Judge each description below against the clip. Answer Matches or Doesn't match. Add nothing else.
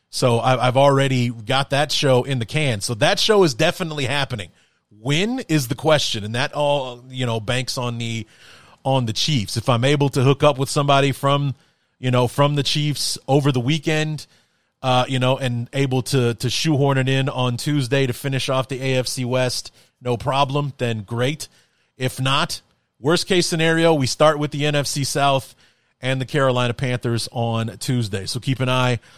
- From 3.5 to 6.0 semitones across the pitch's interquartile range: Doesn't match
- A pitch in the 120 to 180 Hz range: Matches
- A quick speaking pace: Doesn't match